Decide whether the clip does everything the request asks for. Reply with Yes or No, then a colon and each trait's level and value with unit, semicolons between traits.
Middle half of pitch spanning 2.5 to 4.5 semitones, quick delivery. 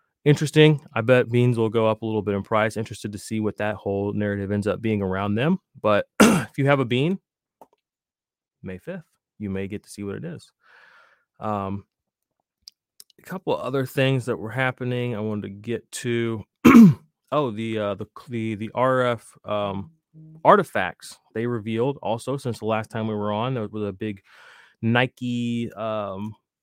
No: average, 3.8 semitones; average, 180 wpm